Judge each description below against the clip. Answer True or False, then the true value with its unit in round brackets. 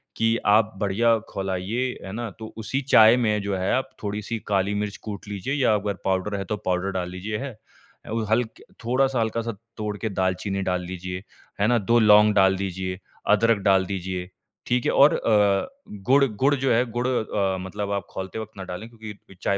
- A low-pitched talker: True (105 Hz)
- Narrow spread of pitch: False (3.0 semitones)